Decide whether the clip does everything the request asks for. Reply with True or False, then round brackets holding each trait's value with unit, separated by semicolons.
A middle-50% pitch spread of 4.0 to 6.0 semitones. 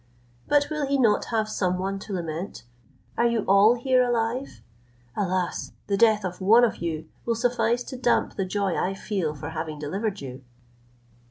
True (4.7 semitones)